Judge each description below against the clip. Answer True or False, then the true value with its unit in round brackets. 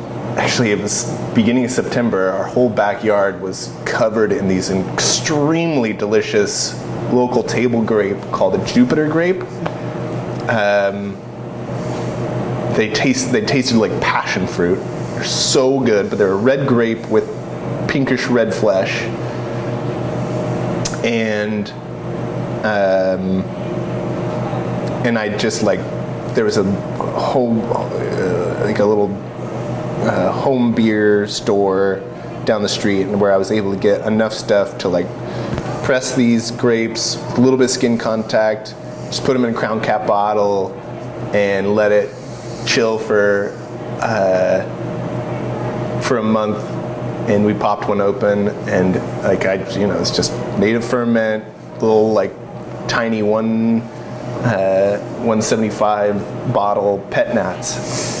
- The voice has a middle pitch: False (110 Hz)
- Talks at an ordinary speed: False (130 wpm)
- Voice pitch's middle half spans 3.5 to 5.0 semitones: False (2.9 semitones)